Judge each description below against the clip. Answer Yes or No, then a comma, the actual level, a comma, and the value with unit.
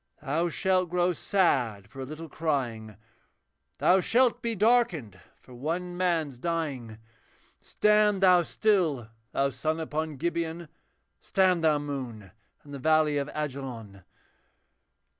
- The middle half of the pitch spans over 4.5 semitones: Yes, average, 5.2 semitones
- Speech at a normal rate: No, slow, 120 wpm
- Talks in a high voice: No, medium, 155 Hz